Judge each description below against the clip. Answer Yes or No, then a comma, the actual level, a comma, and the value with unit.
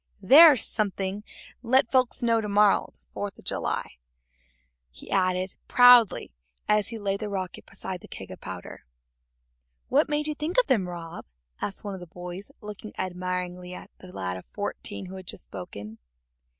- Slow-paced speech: No, average, 170 wpm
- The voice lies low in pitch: No, high, 195 Hz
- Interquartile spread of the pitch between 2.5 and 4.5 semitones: Yes, average, 3.9 semitones